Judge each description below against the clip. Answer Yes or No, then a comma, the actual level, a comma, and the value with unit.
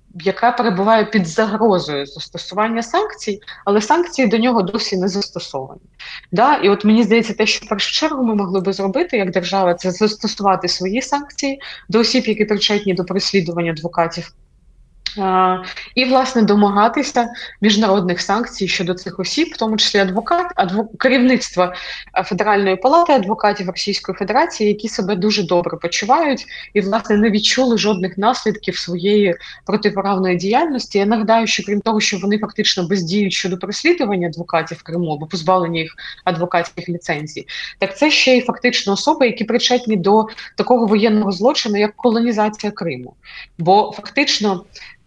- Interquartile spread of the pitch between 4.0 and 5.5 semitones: No, average, 3.4 semitones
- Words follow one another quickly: No, average, 145 wpm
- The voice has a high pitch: Yes, high, 210 Hz